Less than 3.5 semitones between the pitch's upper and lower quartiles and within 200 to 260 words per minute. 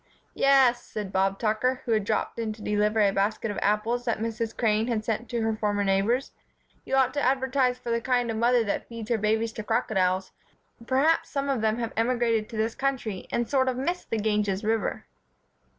Yes: average, 2.8 semitones; fast, 205 wpm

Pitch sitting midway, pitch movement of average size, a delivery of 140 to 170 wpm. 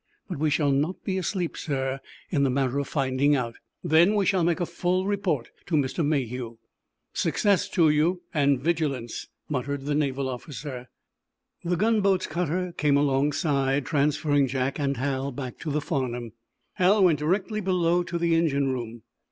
Yes: medium, 150 Hz; average, 4.2 semitones; average, 160 wpm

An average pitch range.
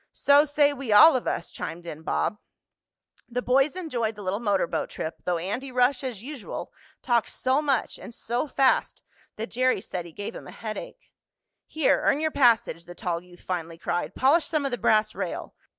No: wide, 6.6 semitones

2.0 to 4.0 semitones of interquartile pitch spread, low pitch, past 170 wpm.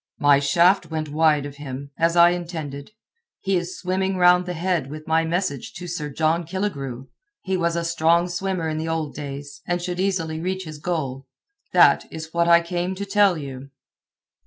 No: average, 3.1 semitones; medium, 170 Hz; average, 185 wpm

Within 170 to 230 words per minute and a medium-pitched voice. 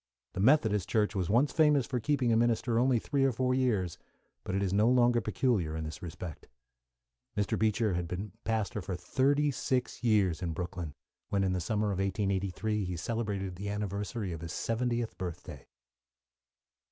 No: average, 175 wpm; low, 105 Hz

